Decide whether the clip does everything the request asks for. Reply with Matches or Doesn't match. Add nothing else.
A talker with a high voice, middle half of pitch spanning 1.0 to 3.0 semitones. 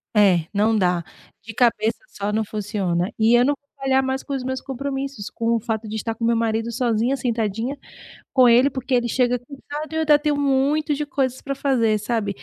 Doesn't match